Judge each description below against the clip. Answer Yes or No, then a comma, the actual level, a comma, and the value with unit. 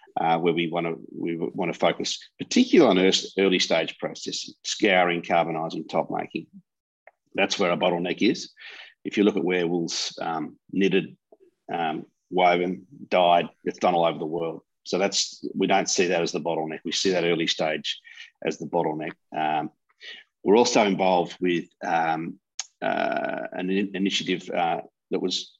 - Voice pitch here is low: Yes, very low, 90 Hz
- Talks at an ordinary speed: Yes, average, 165 wpm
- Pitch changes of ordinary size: No, narrow, 1.8 semitones